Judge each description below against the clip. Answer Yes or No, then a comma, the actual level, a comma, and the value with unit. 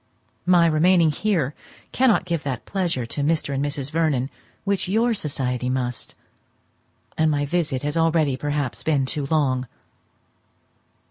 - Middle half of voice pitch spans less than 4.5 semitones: Yes, average, 3.9 semitones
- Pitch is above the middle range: No, medium, 150 Hz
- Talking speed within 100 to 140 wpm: Yes, slow, 135 wpm